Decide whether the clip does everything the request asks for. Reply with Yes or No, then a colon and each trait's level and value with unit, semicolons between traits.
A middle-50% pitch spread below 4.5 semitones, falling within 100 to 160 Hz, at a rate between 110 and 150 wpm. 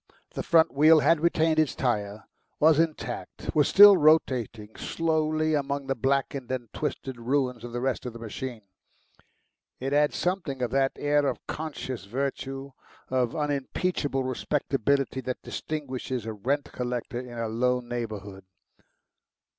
Yes: average, 3.6 semitones; low, 135 Hz; average, 140 wpm